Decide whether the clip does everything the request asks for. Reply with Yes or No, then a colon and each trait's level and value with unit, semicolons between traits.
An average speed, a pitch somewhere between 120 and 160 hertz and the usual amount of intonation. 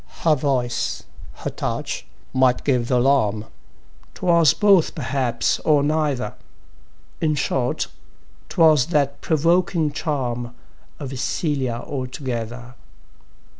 No: slow, 95 wpm; medium, 140 Hz; average, 3.9 semitones